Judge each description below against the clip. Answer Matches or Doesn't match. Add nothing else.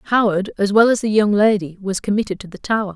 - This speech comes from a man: Doesn't match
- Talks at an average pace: Doesn't match